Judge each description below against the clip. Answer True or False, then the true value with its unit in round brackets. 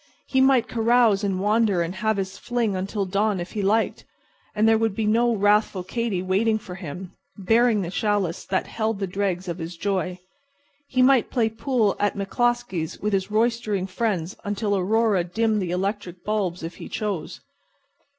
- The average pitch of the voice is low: False (205 Hz)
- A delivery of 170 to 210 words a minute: True (175 wpm)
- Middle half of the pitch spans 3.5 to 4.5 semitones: False (3.1 semitones)